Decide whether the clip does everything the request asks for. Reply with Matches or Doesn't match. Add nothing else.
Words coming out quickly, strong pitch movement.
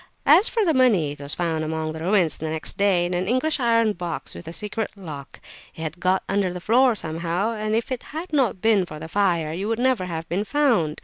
Matches